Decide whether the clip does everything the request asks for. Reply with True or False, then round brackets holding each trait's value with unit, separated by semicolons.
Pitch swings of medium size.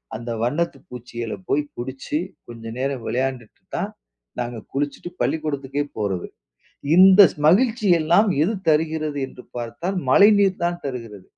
False (6.2 semitones)